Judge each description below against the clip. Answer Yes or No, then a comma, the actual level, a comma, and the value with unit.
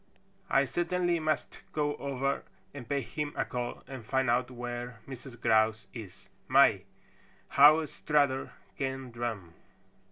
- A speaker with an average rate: No, slow, 130 wpm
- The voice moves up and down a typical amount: Yes, average, 3.1 semitones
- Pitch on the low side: Yes, low, 130 Hz